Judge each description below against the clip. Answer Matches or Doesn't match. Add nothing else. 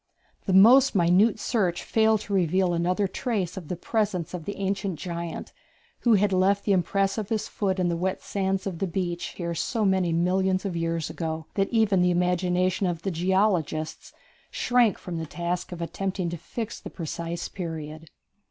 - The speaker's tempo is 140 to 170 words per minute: Doesn't match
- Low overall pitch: Doesn't match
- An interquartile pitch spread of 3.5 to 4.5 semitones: Doesn't match